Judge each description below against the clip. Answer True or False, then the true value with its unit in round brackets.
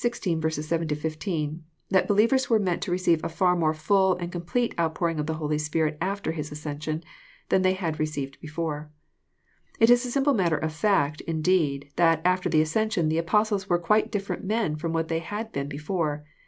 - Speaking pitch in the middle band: True (165 Hz)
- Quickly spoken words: False (170 wpm)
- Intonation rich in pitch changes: False (3.8 semitones)